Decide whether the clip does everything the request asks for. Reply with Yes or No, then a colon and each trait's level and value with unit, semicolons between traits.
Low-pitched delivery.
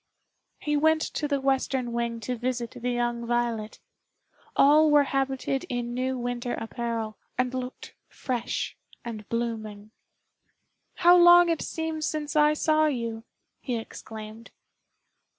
No: very high, 250 Hz